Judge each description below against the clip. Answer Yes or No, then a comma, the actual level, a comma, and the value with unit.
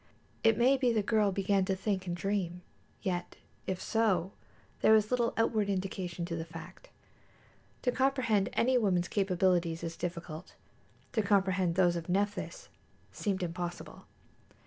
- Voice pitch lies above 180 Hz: Yes, high, 190 Hz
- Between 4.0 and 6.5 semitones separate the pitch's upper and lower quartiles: No, average, 3.6 semitones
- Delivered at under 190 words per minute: Yes, average, 145 wpm